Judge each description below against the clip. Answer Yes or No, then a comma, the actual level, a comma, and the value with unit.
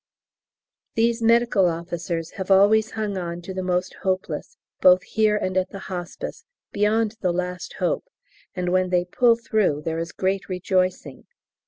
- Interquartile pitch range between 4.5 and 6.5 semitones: No, average, 3.0 semitones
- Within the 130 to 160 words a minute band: Yes, average, 155 wpm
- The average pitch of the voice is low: No, medium, 185 Hz